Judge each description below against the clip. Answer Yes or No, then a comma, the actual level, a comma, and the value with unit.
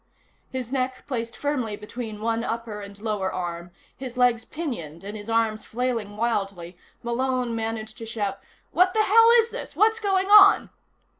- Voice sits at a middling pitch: No, high, 230 Hz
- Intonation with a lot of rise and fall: No, average, 3.7 semitones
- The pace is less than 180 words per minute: Yes, average, 160 wpm